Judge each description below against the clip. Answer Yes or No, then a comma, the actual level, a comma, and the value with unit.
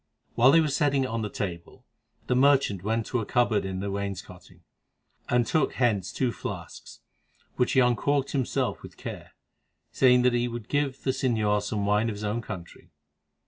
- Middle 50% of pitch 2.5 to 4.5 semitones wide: Yes, average, 4.1 semitones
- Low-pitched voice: Yes, low, 120 Hz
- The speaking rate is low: No, average, 185 wpm